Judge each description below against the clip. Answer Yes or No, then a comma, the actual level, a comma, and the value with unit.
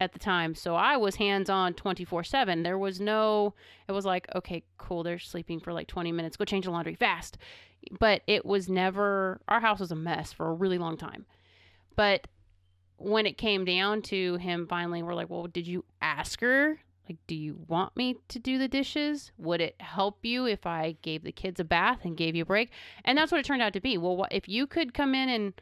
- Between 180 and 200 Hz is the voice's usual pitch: Yes, medium, 185 Hz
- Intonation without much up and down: No, average, 3.6 semitones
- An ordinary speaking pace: No, fast, 230 wpm